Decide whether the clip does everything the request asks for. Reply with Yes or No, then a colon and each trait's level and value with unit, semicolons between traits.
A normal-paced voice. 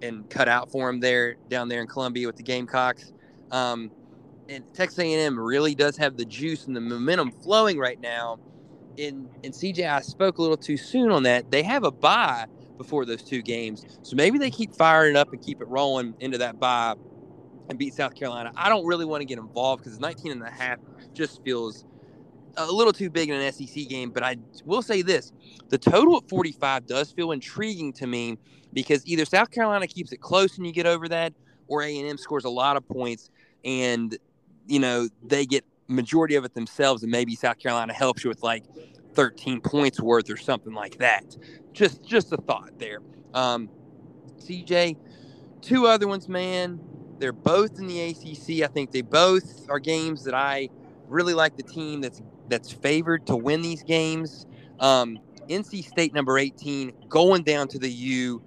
Yes: average, 195 wpm